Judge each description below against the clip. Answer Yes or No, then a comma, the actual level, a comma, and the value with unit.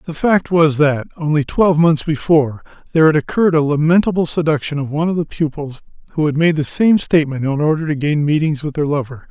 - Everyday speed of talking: No, fast, 215 wpm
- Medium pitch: Yes, medium, 155 Hz